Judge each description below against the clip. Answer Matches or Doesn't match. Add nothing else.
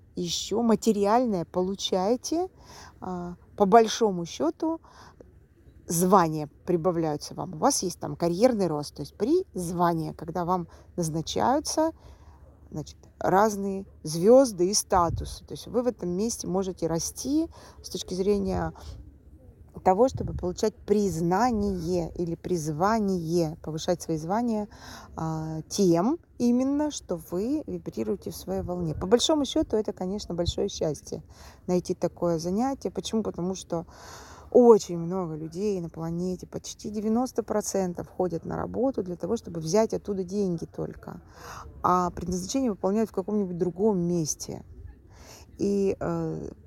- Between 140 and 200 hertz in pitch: Matches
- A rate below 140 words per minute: Matches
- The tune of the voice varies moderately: Matches